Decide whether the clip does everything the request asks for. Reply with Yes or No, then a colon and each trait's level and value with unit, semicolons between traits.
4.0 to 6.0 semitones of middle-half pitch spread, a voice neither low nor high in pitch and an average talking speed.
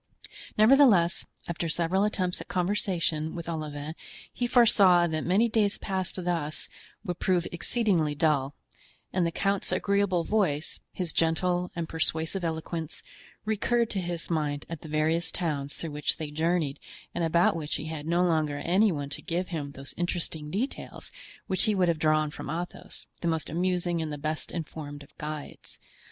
No: average, 2.9 semitones; medium, 170 Hz; average, 165 wpm